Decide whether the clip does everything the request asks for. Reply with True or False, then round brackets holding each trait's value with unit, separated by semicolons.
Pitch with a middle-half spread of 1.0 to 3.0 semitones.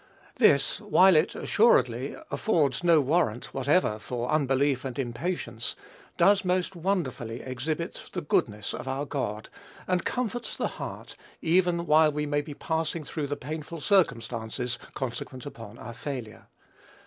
False (5.5 semitones)